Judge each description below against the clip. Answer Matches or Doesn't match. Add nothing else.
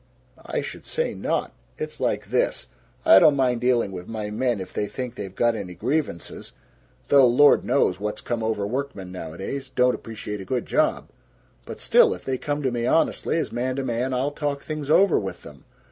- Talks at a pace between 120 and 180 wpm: Doesn't match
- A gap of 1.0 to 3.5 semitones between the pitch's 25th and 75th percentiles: Doesn't match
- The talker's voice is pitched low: Matches